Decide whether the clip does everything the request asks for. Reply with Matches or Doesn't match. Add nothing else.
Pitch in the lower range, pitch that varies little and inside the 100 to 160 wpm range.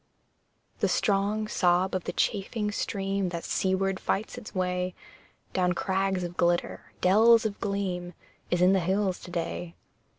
Doesn't match